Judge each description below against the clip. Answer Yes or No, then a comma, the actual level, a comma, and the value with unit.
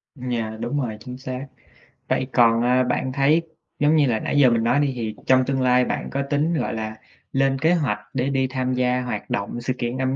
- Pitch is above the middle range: No, low, 130 Hz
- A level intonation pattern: Yes, narrow, 2.2 semitones